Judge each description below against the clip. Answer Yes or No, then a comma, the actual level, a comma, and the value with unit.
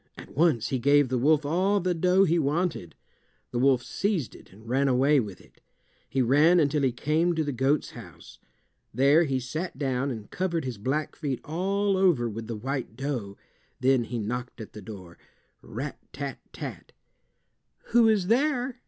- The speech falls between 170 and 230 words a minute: Yes, average, 175 wpm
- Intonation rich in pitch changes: Yes, wide, 5.8 semitones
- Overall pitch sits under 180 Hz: Yes, medium, 140 Hz